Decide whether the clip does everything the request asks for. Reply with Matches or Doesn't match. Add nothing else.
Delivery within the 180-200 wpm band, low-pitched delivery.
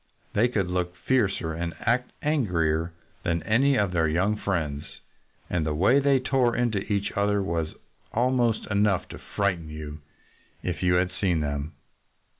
Doesn't match